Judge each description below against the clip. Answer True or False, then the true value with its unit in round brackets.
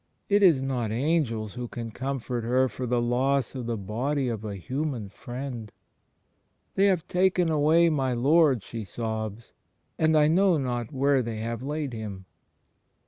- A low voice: True (130 Hz)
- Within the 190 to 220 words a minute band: False (160 wpm)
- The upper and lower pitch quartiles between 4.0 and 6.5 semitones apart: True (4.6 semitones)